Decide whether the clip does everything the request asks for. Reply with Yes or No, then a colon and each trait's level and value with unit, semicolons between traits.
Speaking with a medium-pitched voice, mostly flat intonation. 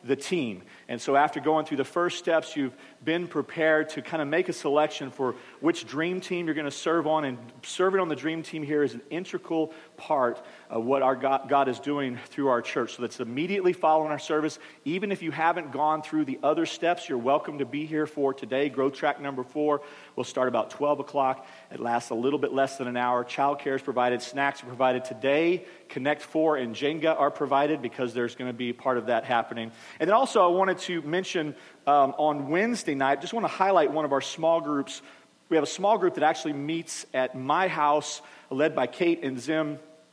No: medium, 150 Hz; average, 3.1 semitones